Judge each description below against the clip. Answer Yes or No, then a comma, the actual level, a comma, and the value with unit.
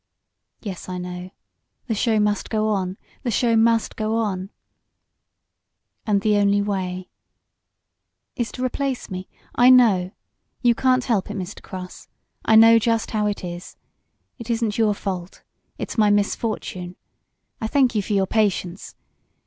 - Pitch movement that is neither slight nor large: Yes, average, 3.3 semitones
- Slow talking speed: No, average, 150 wpm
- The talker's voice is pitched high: Yes, high, 210 Hz